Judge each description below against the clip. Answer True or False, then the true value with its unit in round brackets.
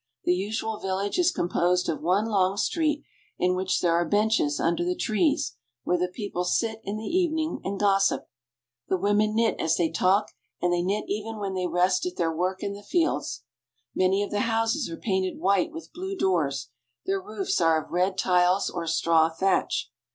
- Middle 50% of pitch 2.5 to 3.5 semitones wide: True (3.2 semitones)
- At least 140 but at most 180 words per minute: False (190 wpm)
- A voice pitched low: False (190 Hz)